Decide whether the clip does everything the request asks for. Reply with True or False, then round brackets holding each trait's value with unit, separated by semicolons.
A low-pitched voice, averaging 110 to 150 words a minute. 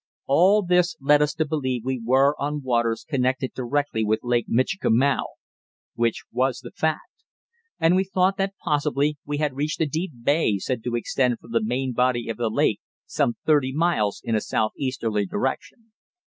False (130 Hz; 175 wpm)